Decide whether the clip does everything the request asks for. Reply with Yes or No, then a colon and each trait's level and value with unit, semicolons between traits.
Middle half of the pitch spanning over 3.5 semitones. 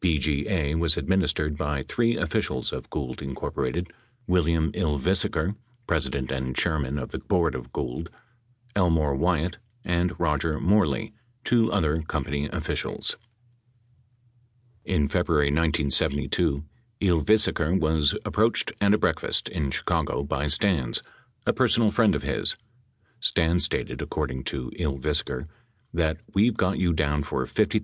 Yes: average, 4.1 semitones